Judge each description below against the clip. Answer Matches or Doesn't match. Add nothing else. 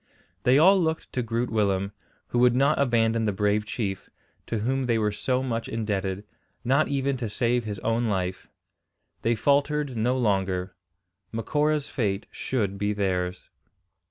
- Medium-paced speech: Matches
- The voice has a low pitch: Matches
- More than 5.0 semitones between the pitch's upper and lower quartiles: Doesn't match